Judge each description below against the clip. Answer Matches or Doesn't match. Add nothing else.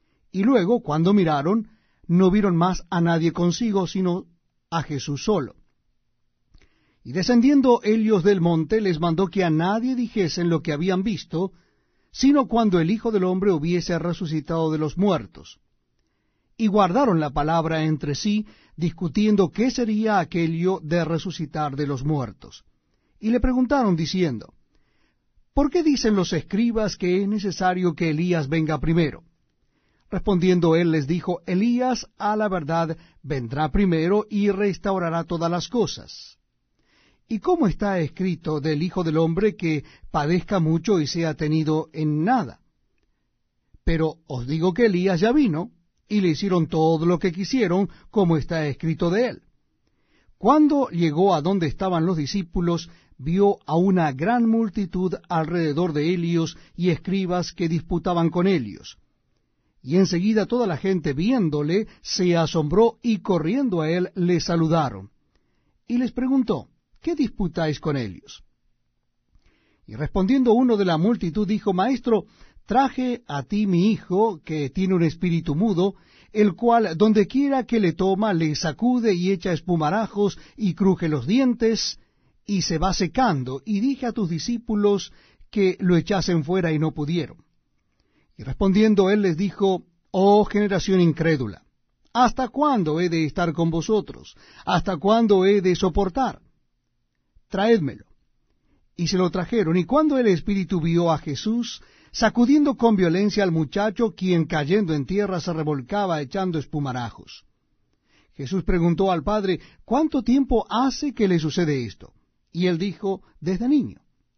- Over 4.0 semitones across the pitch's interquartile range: Matches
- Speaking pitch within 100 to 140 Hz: Doesn't match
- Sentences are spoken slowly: Doesn't match